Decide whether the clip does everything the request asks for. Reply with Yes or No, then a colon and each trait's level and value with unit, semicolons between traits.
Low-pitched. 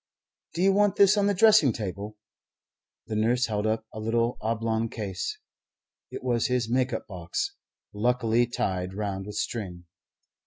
Yes: low, 115 Hz